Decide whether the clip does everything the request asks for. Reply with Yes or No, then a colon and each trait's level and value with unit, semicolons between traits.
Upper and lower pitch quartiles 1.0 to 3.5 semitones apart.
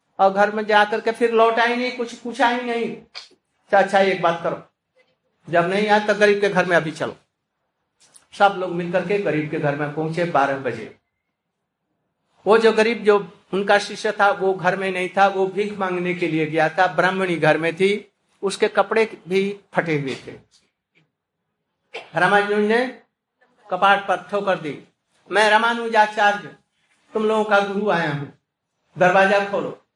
Yes: average, 3.1 semitones